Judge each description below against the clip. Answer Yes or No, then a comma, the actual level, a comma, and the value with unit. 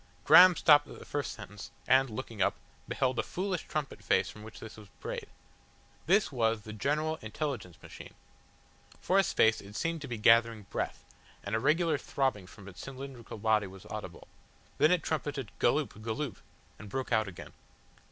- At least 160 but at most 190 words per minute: Yes, average, 175 wpm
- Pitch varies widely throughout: Yes, wide, 5.7 semitones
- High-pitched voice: No, low, 125 Hz